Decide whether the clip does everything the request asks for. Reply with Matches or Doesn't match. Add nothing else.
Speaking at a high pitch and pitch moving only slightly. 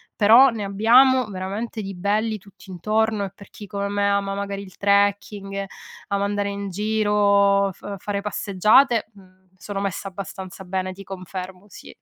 Matches